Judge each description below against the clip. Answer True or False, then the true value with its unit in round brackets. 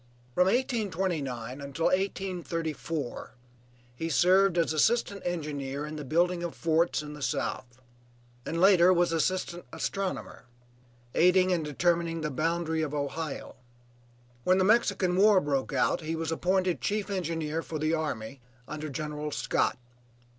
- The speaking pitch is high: False (165 Hz)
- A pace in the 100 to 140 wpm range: True (135 wpm)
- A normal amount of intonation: True (3.4 semitones)